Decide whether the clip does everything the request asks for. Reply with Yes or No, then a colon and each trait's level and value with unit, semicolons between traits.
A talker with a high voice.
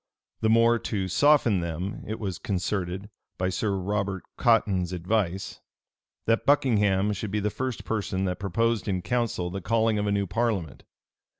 No: low, 100 Hz